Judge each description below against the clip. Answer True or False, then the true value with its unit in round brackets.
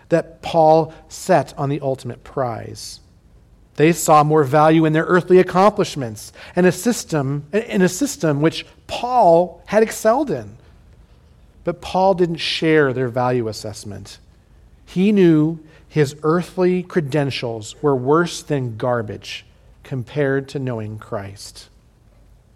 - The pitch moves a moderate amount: False (6.6 semitones)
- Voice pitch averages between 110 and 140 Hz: False (150 Hz)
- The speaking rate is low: True (120 wpm)